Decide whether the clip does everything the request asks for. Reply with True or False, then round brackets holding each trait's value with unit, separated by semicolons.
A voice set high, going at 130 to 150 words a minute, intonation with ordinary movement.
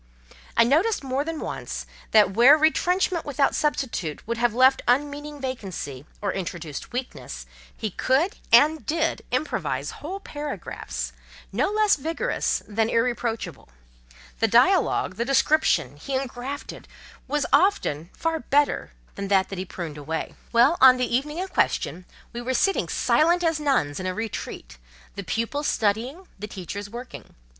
False (255 Hz; 140 wpm; 6.9 semitones)